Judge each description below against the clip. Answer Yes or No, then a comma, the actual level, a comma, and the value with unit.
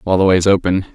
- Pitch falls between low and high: No, very low, 95 Hz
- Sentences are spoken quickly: Yes, fast, 255 wpm